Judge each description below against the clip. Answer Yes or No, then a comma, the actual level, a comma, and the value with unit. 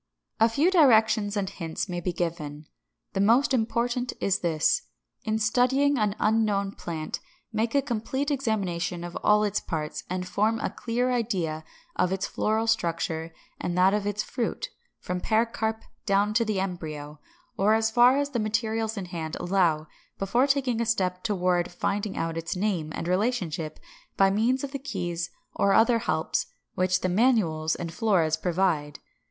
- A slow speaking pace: No, average, 165 wpm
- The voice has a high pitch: Yes, high, 200 Hz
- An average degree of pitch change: Yes, average, 4.5 semitones